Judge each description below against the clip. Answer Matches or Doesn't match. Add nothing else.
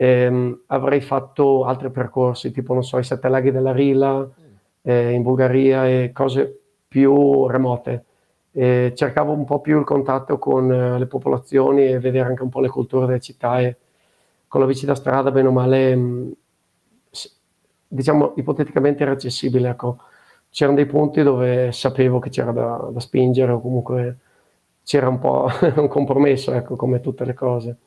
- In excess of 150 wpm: Matches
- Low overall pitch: Matches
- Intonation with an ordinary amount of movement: Doesn't match